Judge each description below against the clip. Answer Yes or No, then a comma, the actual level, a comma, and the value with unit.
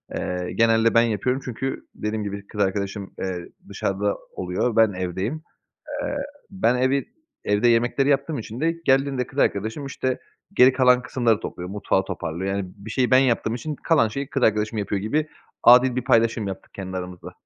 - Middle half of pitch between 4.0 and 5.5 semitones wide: Yes, average, 4.5 semitones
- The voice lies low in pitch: Yes, low, 115 Hz